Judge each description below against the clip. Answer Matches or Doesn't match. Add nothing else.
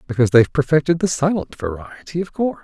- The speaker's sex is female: Doesn't match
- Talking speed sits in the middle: Matches